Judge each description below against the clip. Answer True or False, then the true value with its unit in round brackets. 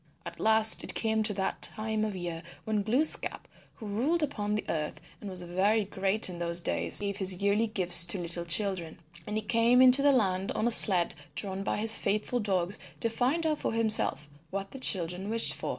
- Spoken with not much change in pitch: False (3.2 semitones)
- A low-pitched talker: False (205 Hz)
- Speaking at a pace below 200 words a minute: False (205 wpm)